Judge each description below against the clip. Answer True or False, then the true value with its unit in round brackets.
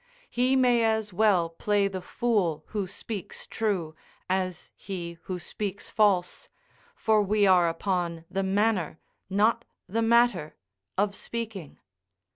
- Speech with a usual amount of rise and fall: True (3.6 semitones)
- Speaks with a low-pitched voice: False (200 Hz)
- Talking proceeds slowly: True (125 wpm)